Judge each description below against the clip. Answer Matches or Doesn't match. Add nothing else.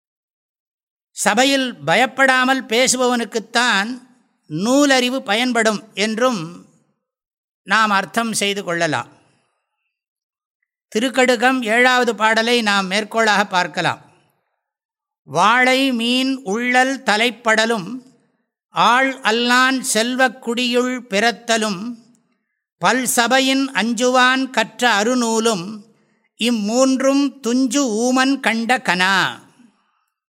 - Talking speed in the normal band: Doesn't match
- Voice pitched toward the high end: Matches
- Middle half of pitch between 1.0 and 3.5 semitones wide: Matches